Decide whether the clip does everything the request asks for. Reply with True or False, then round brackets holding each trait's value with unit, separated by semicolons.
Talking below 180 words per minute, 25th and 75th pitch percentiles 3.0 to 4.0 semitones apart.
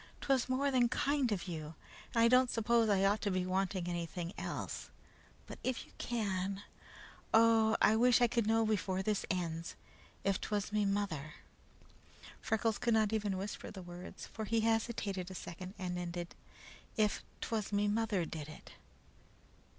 True (165 wpm; 3.5 semitones)